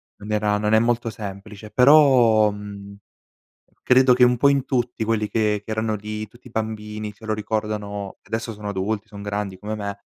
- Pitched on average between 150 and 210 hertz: No, low, 110 Hz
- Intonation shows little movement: Yes, narrow, 1.6 semitones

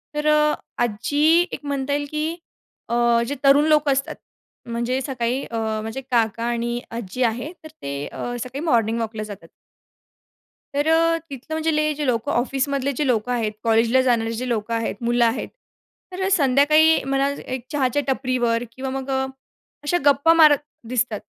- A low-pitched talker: No, very high, 260 Hz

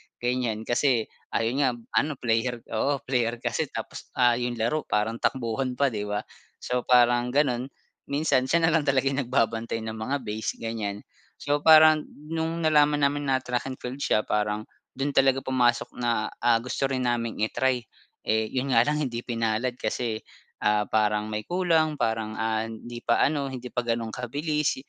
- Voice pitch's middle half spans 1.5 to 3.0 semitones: No, average, 3.5 semitones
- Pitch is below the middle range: Yes, low, 125 Hz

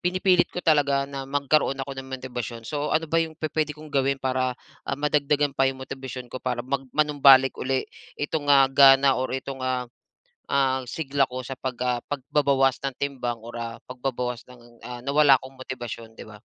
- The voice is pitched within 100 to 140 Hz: Yes, low, 135 Hz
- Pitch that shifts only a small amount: Yes, narrow, 2.1 semitones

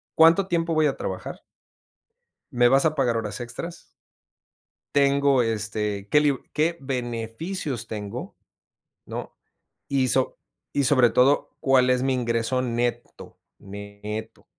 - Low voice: Yes, low, 125 Hz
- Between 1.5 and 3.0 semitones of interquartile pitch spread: No, average, 3.9 semitones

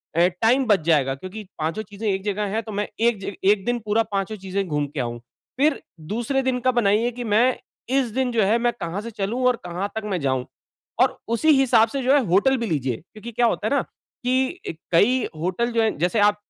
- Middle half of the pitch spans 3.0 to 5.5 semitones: Yes, average, 4.5 semitones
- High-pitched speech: Yes, high, 215 Hz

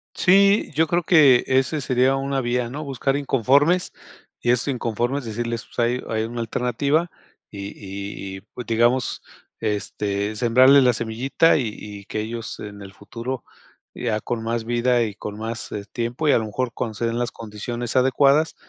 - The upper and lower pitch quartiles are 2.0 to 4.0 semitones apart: Yes, average, 3.2 semitones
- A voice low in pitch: Yes, low, 120 Hz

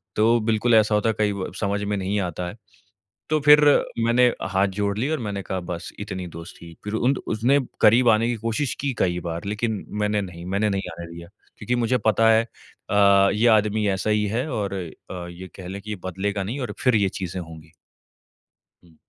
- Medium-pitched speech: No, low, 105 Hz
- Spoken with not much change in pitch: No, average, 3.2 semitones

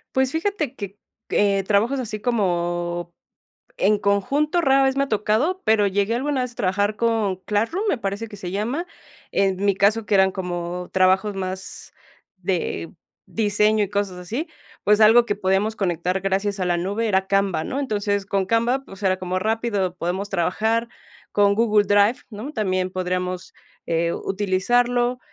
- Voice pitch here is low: No, high, 205 Hz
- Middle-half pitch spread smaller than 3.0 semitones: No, average, 3.5 semitones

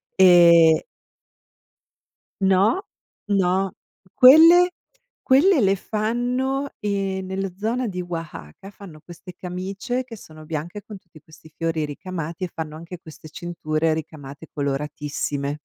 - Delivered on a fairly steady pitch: No, average, 4.7 semitones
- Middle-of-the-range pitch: Yes, medium, 180 Hz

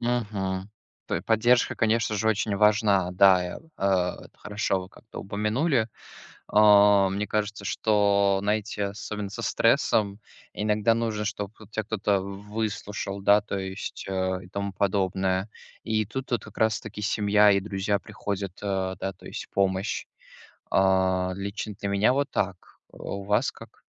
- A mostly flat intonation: Yes, narrow, 1.7 semitones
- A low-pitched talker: Yes, low, 100 Hz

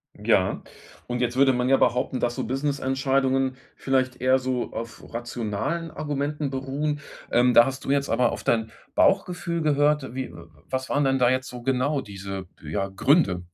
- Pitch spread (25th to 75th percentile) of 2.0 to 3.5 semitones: Yes, narrow, 2.4 semitones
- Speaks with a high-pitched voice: No, low, 130 Hz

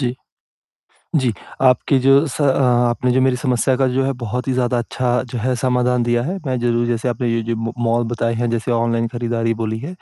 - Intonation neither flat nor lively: No, narrow, 1.7 semitones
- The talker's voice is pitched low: Yes, low, 120 Hz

